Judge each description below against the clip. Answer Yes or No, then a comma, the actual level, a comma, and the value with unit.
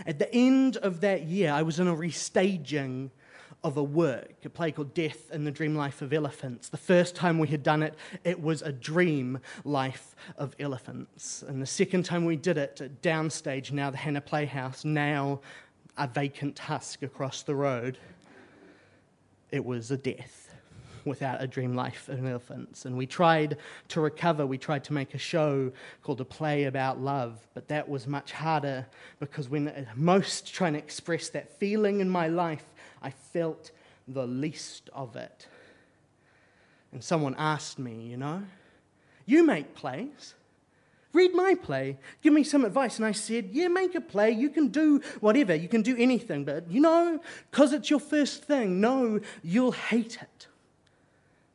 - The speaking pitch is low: No, medium, 155 Hz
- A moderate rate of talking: Yes, average, 170 wpm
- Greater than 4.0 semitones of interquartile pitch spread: Yes, average, 5.3 semitones